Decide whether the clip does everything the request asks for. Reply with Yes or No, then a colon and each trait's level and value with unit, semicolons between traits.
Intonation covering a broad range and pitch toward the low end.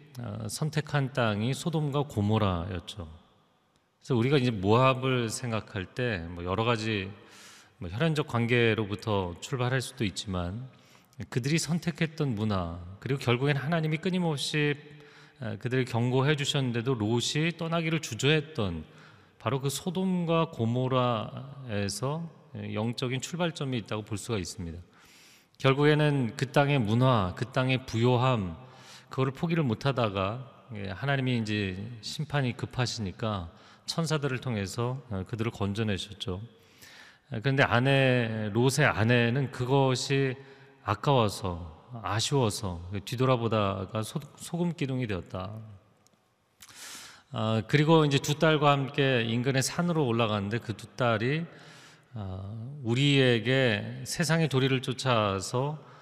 No: average, 4.7 semitones; low, 125 Hz